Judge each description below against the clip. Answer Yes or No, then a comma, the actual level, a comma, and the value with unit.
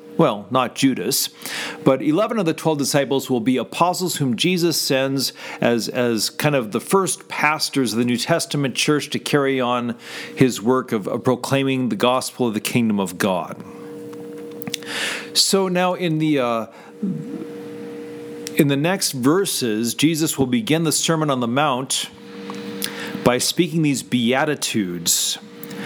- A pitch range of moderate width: Yes, average, 4.2 semitones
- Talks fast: No, average, 145 wpm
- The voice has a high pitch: No, medium, 140 Hz